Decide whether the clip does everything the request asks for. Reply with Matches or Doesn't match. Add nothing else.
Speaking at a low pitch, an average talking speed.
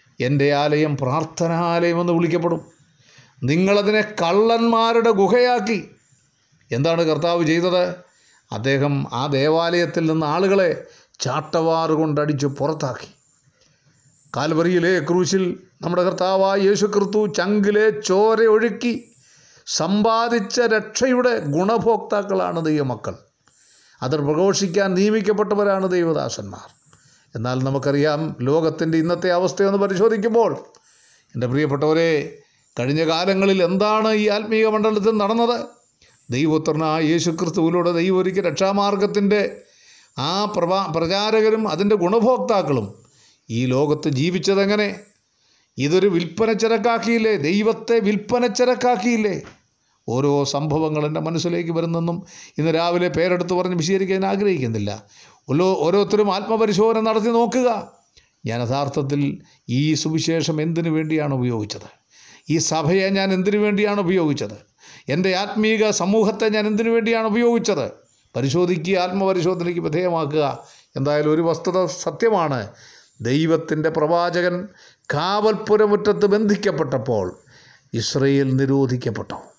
Doesn't match